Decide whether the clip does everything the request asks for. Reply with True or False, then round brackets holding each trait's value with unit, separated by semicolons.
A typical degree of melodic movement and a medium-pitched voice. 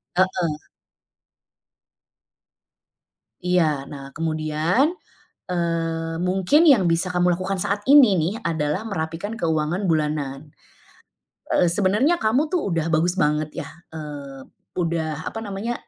True (4.0 semitones; 170 Hz)